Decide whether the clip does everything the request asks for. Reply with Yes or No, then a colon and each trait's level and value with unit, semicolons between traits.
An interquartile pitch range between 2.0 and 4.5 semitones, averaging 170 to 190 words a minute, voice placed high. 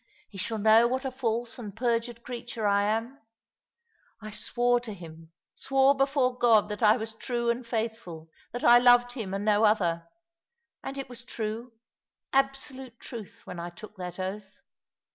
Yes: average, 2.9 semitones; average, 175 wpm; high, 230 Hz